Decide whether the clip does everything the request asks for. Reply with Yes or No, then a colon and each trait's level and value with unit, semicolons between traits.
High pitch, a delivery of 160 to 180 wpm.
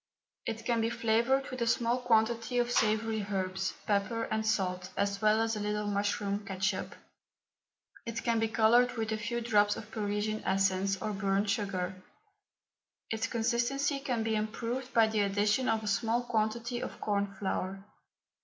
Yes: high, 220 Hz; average, 165 wpm